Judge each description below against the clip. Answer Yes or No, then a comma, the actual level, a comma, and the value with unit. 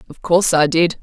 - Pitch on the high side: No, medium, 165 Hz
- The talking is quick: Yes, fast, 235 wpm